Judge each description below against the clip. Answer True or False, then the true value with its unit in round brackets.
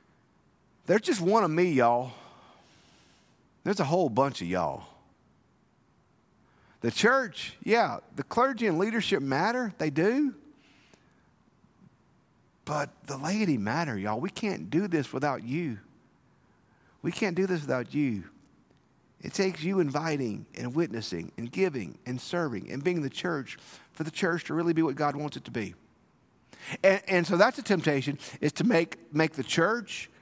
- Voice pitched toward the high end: False (165 Hz)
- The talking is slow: False (155 wpm)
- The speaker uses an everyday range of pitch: False (5.9 semitones)